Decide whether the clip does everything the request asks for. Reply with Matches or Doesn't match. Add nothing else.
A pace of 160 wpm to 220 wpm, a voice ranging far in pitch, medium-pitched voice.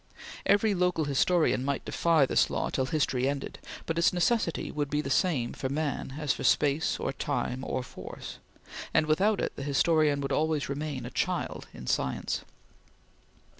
Doesn't match